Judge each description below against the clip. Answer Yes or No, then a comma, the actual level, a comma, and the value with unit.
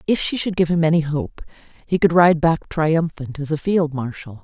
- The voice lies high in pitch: No, medium, 160 Hz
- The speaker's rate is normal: No, fast, 215 wpm